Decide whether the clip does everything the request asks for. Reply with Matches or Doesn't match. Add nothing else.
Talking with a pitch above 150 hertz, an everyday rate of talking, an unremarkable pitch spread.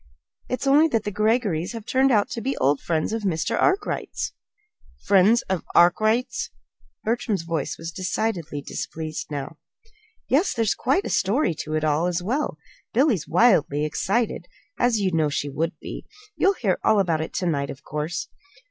Doesn't match